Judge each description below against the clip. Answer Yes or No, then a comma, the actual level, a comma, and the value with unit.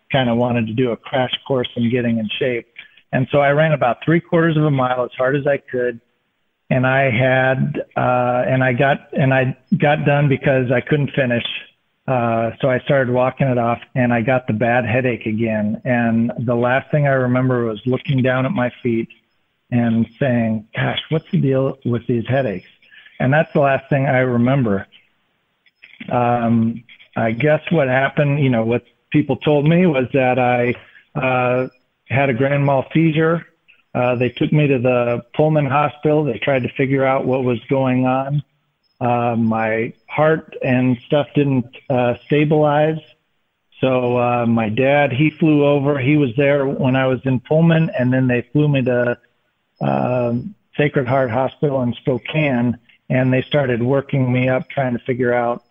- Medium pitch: No, low, 130 Hz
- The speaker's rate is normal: Yes, average, 180 wpm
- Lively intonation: No, average, 2.9 semitones